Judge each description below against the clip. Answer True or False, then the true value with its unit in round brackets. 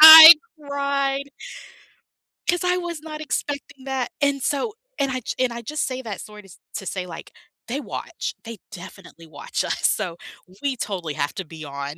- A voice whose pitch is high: True (260 Hz)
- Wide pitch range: True (7.2 semitones)